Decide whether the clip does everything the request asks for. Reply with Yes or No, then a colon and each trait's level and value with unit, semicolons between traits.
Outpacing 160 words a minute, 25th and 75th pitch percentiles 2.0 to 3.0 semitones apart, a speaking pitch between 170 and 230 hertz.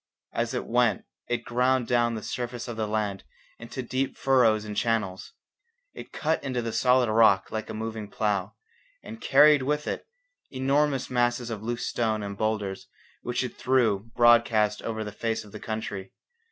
No: average, 170 wpm; narrow, 2.6 semitones; low, 115 Hz